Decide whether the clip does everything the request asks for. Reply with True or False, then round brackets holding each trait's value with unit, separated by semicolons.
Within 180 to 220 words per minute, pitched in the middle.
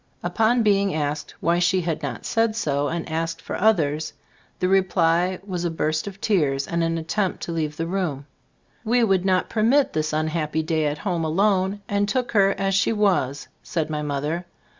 True (190 wpm; 175 Hz)